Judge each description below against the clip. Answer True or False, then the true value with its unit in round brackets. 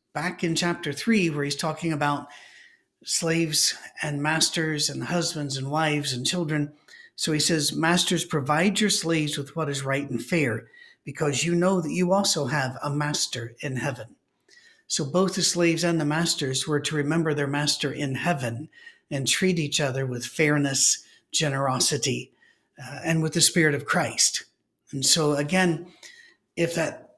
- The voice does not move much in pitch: False (3.2 semitones)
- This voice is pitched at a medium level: True (155 Hz)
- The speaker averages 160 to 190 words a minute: True (165 wpm)